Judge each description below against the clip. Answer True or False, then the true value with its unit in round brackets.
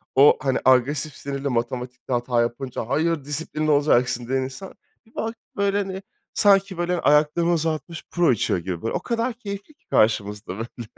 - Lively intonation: True (6.4 semitones)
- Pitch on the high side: False (145 Hz)